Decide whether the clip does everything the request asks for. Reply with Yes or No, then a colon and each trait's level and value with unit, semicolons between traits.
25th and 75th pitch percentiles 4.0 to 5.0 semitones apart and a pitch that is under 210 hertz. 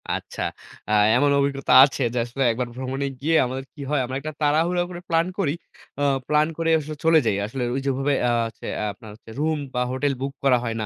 No: average, 3.2 semitones; medium, 140 Hz